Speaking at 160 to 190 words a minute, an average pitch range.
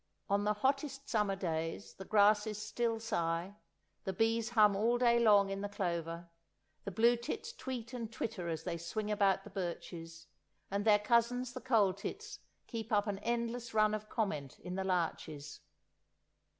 Yes: average, 165 wpm; average, 3.6 semitones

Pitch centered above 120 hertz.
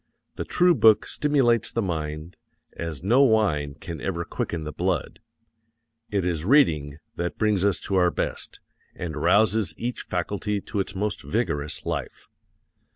No: very low, 95 Hz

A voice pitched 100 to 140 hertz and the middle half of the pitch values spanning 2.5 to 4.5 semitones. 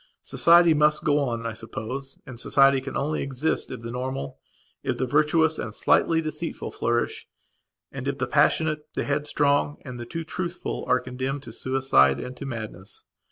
Yes: low, 135 Hz; average, 3.9 semitones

